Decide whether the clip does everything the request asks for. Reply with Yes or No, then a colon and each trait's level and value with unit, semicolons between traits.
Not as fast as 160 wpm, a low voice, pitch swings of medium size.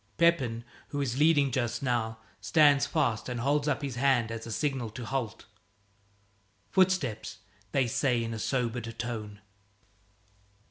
Yes: average, 140 wpm; low, 125 Hz; average, 3.5 semitones